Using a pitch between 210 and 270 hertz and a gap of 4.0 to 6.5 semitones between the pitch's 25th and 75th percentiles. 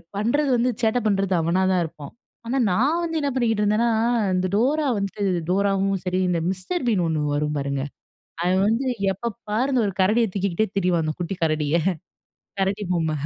No: high, 195 Hz; average, 4.8 semitones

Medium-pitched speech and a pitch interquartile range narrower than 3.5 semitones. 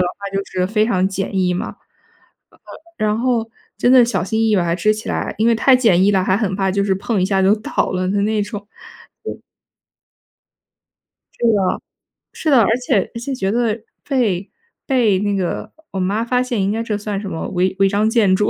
No: high, 205 Hz; average, 3.0 semitones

